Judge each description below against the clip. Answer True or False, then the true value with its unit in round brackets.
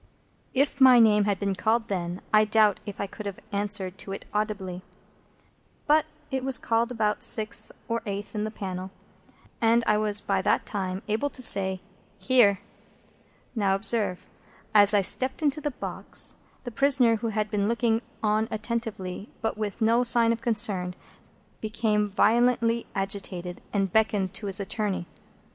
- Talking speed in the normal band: True (160 wpm)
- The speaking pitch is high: True (215 Hz)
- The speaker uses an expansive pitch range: False (2.8 semitones)